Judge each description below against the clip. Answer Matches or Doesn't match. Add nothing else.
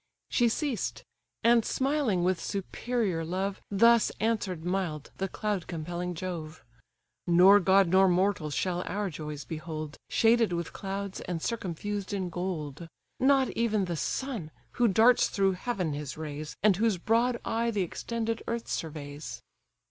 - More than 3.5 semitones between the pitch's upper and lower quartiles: Matches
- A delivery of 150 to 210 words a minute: Doesn't match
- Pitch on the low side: Doesn't match